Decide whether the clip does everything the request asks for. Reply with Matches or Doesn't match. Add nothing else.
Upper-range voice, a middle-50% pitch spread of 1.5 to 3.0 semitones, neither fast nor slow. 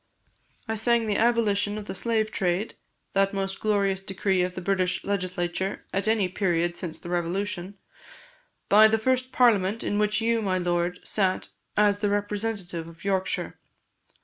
Matches